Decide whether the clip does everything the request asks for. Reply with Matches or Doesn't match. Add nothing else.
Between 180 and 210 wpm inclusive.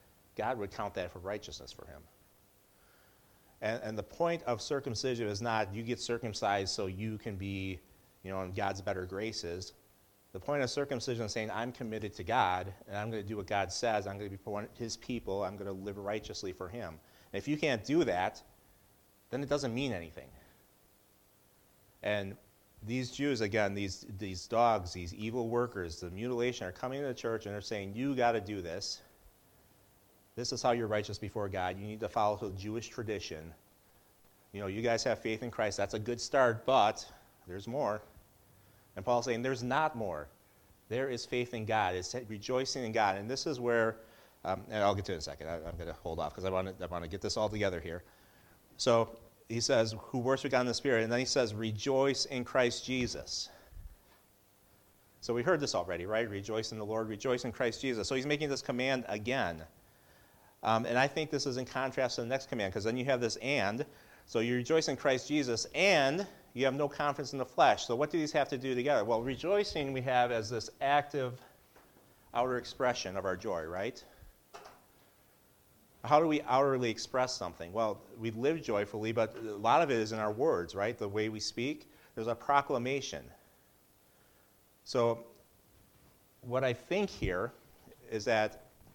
Matches